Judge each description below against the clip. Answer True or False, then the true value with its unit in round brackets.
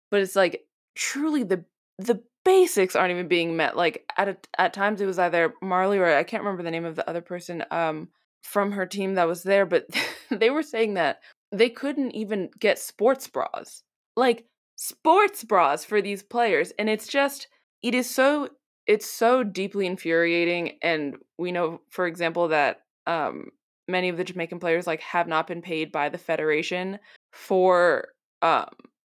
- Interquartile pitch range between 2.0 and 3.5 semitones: False (5.1 semitones)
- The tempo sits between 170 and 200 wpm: True (180 wpm)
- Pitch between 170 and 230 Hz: True (190 Hz)